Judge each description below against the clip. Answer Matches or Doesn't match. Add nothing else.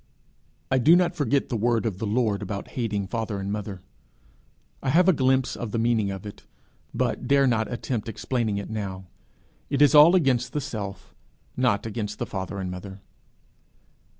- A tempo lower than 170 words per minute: Doesn't match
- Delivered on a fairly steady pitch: Doesn't match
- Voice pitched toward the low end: Matches